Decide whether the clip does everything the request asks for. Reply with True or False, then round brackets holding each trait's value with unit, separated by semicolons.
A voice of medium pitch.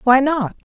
False (260 Hz)